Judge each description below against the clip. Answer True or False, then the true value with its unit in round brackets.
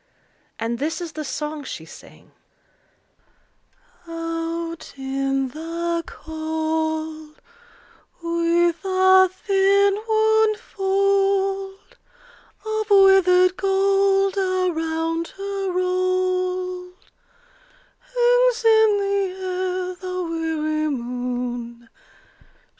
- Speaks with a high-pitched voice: True (365 Hz)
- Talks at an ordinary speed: False (75 wpm)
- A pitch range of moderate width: True (3.5 semitones)